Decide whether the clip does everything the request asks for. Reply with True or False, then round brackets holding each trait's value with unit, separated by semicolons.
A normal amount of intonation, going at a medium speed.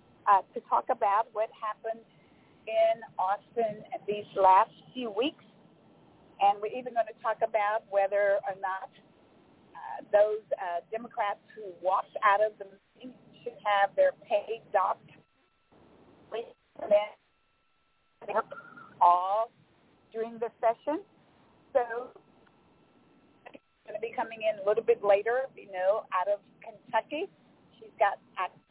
False (4.1 semitones; 120 wpm)